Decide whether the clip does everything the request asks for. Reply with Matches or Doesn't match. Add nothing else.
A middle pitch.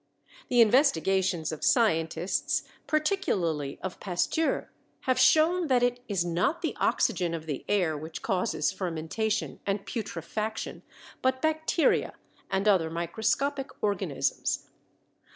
Doesn't match